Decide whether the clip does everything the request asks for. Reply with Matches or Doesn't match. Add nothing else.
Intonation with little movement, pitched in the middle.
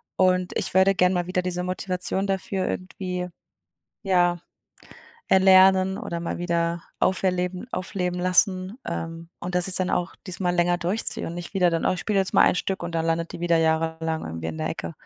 Matches